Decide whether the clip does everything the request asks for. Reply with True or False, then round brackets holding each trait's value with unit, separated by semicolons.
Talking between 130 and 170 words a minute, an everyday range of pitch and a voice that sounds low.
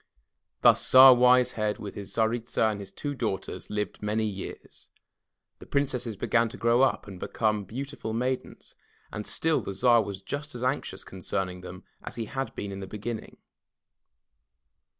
False (185 wpm; 3.8 semitones; 110 Hz)